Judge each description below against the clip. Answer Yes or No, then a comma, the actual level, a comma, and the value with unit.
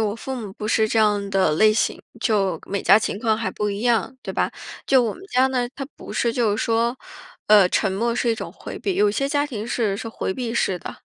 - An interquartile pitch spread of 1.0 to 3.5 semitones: Yes, average, 2.8 semitones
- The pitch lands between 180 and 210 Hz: No, high, 220 Hz